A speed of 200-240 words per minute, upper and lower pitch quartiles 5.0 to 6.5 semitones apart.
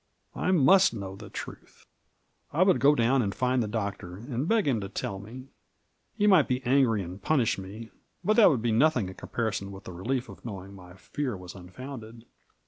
Yes: fast, 205 wpm; wide, 5.6 semitones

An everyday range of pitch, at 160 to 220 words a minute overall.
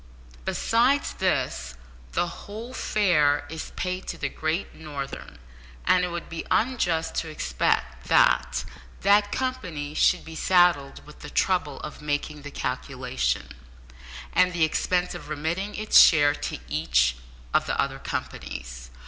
No: average, 4.2 semitones; average, 140 wpm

